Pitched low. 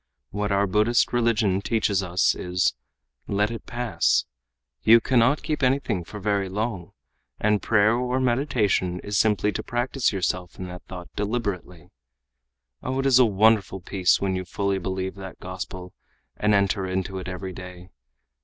Yes: low, 100 Hz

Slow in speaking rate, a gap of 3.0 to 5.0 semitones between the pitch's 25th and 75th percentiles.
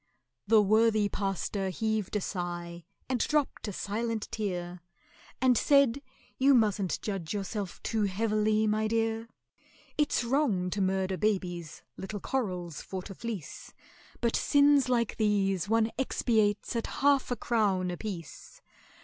Yes: slow, 130 wpm; average, 3.4 semitones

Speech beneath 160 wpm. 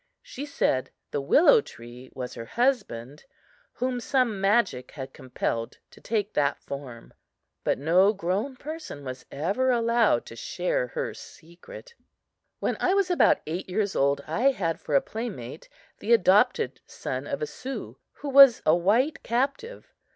Yes: average, 150 wpm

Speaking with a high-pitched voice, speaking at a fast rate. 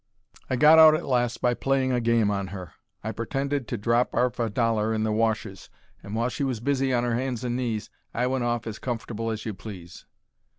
No: low, 115 Hz; fast, 220 wpm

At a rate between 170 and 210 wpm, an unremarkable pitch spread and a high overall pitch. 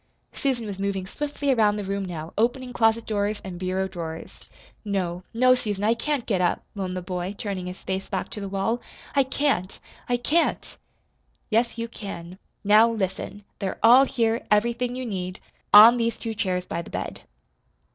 Yes: average, 175 wpm; average, 3.8 semitones; high, 210 Hz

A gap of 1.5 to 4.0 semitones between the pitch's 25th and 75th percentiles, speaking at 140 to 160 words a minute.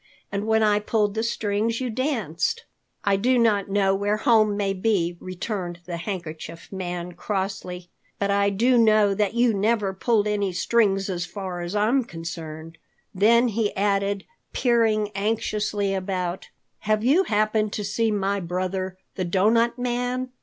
Yes: average, 2.9 semitones; average, 155 wpm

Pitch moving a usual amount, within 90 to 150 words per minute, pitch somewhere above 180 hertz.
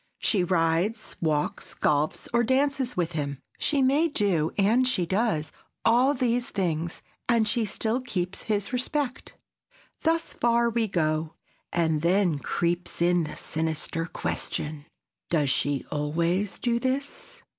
No: wide, 6.7 semitones; slow, 135 wpm; high, 190 Hz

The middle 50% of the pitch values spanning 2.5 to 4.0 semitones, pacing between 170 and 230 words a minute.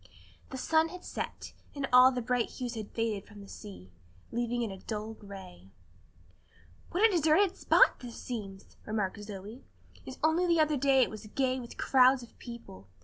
No: average, 4.5 semitones; average, 180 wpm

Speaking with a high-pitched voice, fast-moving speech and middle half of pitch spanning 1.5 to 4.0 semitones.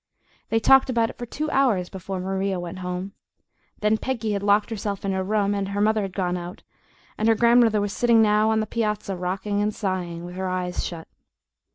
Yes: high, 205 Hz; fast, 210 wpm; average, 2.8 semitones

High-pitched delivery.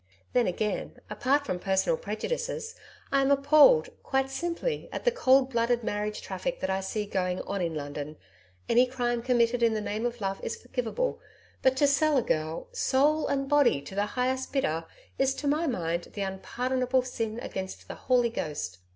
Yes: high, 245 Hz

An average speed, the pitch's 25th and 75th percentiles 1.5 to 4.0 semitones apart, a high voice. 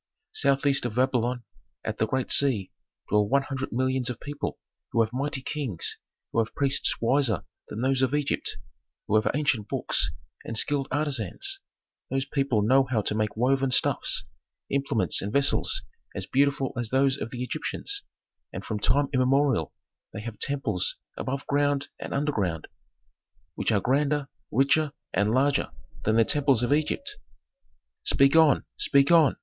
No: average, 155 wpm; average, 3.6 semitones; low, 135 Hz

